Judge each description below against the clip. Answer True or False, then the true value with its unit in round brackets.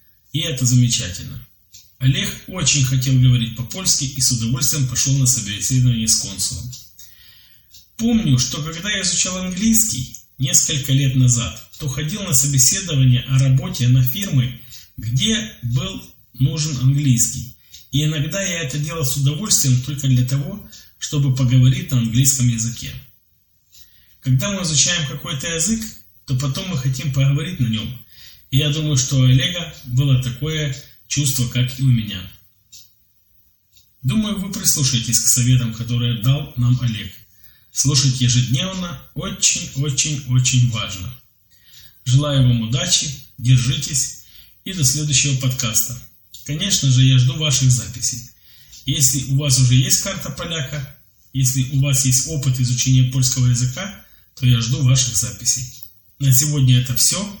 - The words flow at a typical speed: True (135 wpm)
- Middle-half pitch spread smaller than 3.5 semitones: True (2.9 semitones)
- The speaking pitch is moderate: False (130 Hz)